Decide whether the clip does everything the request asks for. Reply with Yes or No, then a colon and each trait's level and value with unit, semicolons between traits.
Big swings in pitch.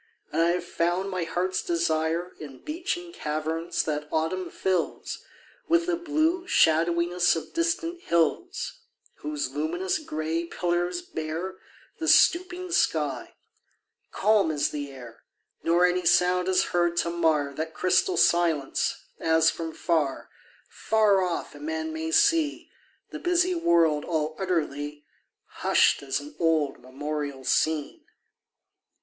Yes: wide, 5.7 semitones